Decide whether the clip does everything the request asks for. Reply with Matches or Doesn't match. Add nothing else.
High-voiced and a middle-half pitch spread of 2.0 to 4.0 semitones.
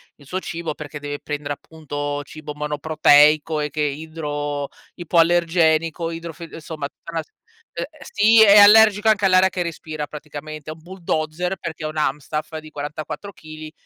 Doesn't match